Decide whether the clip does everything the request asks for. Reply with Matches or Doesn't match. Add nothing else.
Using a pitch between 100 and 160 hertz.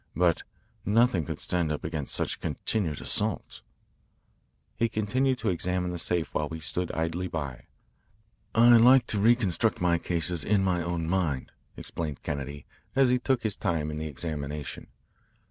Doesn't match